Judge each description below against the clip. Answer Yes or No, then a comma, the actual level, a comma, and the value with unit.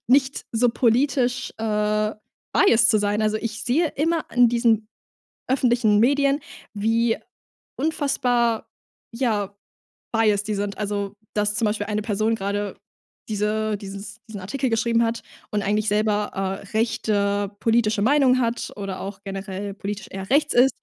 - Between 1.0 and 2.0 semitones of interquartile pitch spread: No, narrow, 2.6 semitones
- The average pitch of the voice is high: Yes, high, 220 Hz